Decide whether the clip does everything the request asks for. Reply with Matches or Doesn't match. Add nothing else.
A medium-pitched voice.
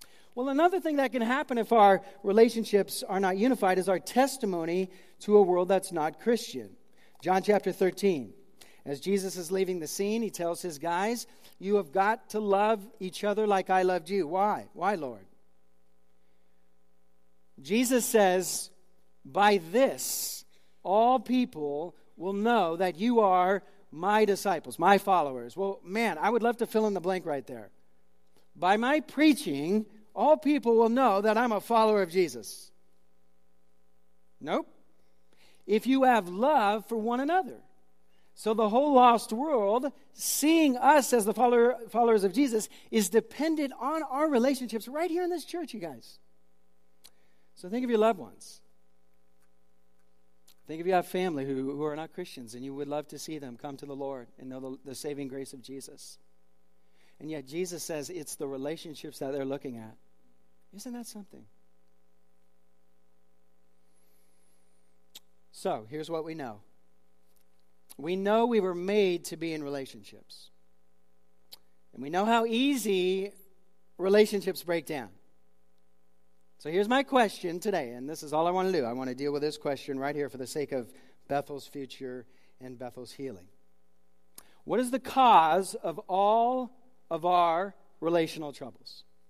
Matches